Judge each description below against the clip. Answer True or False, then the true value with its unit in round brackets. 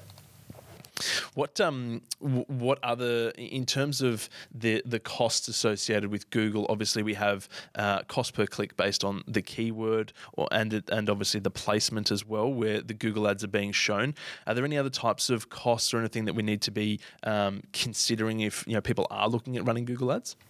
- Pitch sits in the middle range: False (110 Hz)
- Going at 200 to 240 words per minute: False (190 wpm)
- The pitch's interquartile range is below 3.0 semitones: True (2.4 semitones)